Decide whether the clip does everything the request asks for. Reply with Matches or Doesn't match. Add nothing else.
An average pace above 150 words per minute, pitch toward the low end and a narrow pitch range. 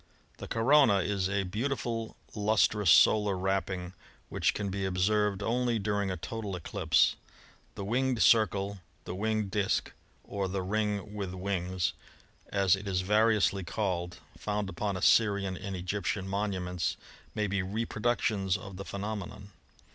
Doesn't match